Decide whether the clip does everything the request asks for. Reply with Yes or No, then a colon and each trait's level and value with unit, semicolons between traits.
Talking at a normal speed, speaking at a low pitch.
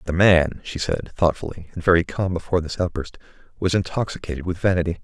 Yes: average, 180 wpm; very low, 85 Hz